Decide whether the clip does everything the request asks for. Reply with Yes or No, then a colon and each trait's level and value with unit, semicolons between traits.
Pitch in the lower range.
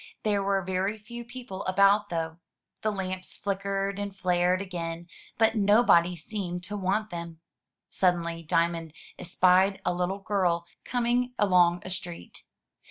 No: high, 190 Hz